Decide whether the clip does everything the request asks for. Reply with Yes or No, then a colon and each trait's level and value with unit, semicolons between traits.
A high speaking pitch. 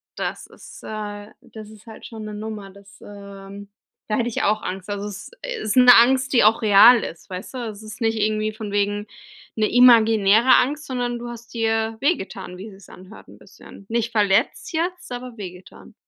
Yes: high, 215 Hz